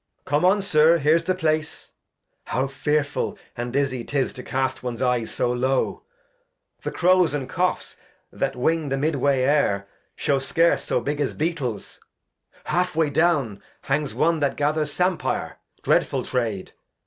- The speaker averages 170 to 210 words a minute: No, average, 160 wpm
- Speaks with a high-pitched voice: No, medium, 145 Hz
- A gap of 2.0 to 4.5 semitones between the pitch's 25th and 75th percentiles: Yes, average, 3.8 semitones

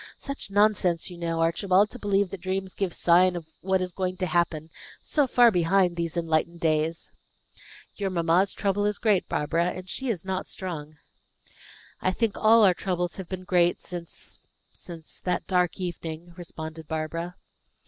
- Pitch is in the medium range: Yes, medium, 180 Hz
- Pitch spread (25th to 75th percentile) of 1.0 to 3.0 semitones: Yes, narrow, 2.4 semitones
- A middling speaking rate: Yes, average, 165 wpm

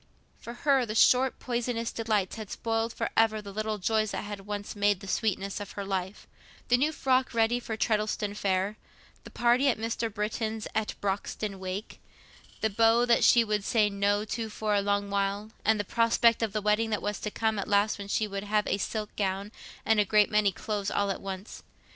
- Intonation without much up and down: Yes, narrow, 1.9 semitones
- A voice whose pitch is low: No, high, 210 Hz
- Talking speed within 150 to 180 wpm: No, fast, 205 wpm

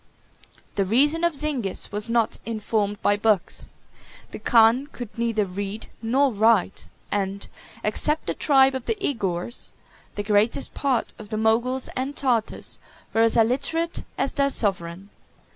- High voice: Yes, high, 225 Hz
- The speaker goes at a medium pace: Yes, average, 145 wpm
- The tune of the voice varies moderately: Yes, average, 4.5 semitones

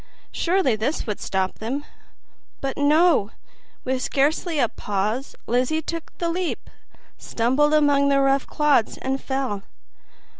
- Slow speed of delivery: Yes, slow, 125 wpm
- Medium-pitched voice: No, very high, 275 Hz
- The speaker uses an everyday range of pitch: Yes, average, 3.9 semitones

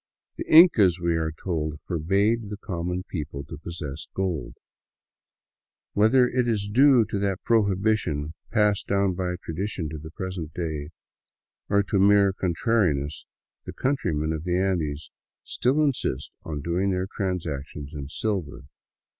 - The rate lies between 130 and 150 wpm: Yes, average, 140 wpm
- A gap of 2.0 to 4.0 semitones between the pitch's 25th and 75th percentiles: No, average, 4.6 semitones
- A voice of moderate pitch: No, very low, 90 Hz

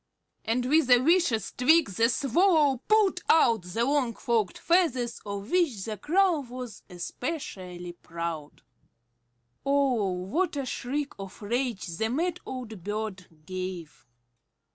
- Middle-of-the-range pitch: No, high, 240 Hz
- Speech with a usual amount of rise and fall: No, wide, 7.0 semitones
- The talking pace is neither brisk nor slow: No, slow, 125 wpm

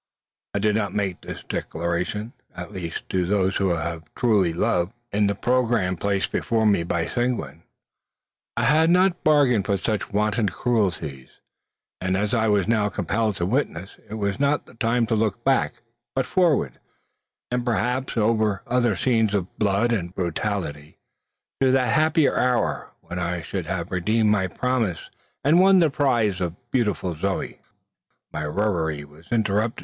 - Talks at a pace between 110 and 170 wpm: Yes, average, 155 wpm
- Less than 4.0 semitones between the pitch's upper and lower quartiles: No, average, 4.8 semitones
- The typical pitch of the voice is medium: No, low, 105 Hz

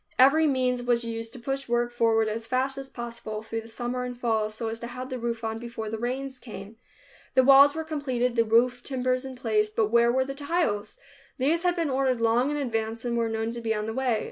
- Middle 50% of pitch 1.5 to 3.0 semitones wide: Yes, narrow, 2.6 semitones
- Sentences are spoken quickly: Yes, fast, 240 wpm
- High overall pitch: Yes, high, 240 Hz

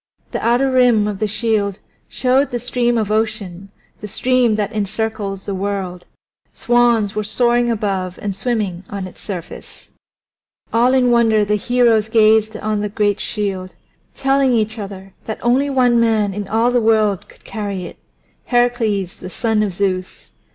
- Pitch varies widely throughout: No, average, 3.1 semitones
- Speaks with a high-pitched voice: Yes, high, 215 Hz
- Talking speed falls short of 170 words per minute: Yes, average, 160 wpm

